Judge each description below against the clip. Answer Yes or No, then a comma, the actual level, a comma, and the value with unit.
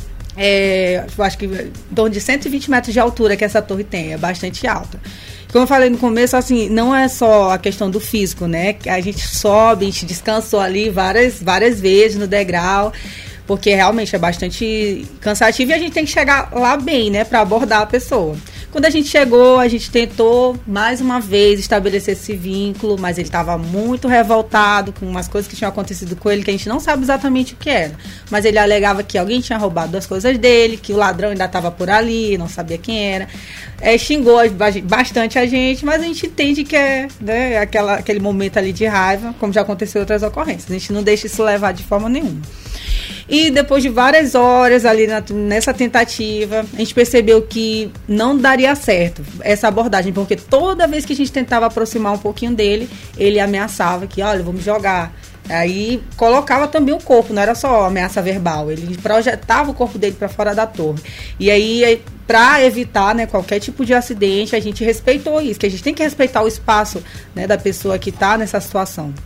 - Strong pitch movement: No, average, 3.7 semitones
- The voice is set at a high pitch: Yes, high, 215 Hz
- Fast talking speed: Yes, fast, 205 wpm